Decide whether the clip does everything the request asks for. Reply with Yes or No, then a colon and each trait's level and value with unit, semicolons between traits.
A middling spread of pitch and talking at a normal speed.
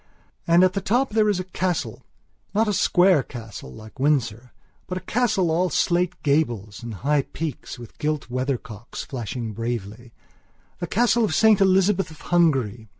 No: wide, 7.6 semitones; average, 150 wpm